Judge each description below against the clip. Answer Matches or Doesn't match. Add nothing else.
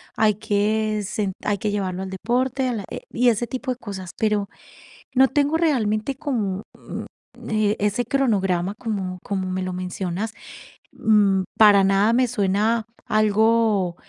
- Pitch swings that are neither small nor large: Matches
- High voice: Matches